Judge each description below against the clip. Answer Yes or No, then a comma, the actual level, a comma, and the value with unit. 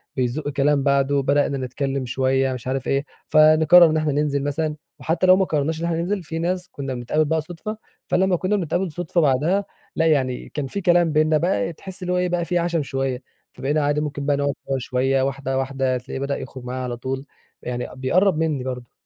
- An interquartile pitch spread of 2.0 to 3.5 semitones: No, average, 3.9 semitones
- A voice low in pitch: No, medium, 145 Hz